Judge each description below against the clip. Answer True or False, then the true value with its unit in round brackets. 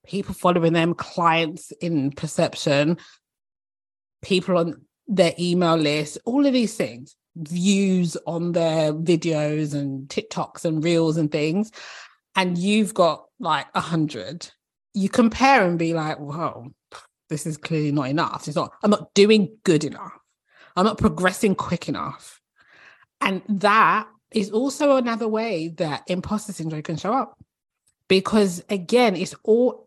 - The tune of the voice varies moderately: True (4.3 semitones)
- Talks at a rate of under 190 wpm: True (140 wpm)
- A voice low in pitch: False (175 Hz)